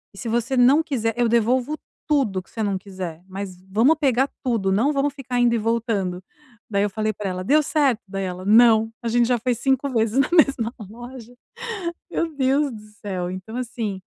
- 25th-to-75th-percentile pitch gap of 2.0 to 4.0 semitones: No, average, 4.6 semitones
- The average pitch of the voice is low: No, high, 230 Hz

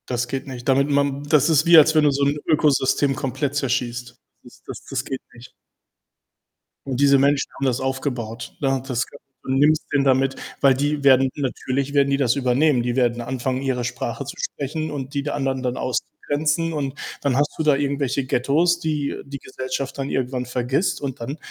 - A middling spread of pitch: No, narrow, 1.9 semitones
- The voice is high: No, low, 135 Hz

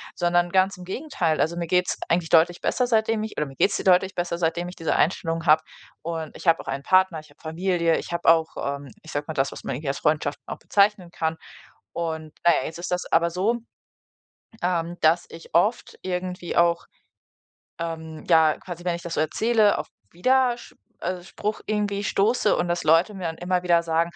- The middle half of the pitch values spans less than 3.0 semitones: Yes, narrow, 2.5 semitones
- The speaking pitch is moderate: Yes, medium, 175 Hz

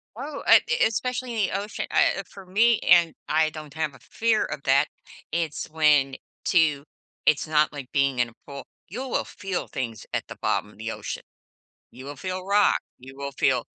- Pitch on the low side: No, medium, 155 Hz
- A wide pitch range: Yes, wide, 6.3 semitones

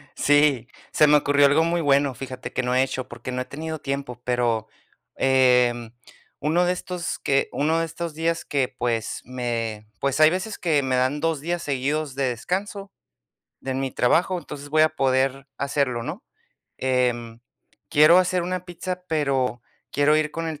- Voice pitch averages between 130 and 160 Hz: Yes, medium, 140 Hz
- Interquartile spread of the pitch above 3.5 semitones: Yes, average, 4.1 semitones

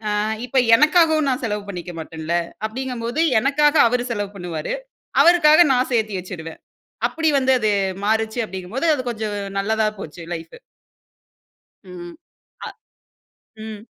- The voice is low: No, high, 220 Hz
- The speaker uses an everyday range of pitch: No, wide, 6.1 semitones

